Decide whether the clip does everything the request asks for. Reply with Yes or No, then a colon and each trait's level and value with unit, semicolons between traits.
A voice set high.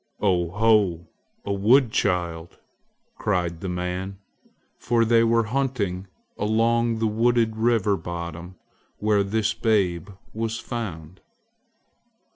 No: low, 105 Hz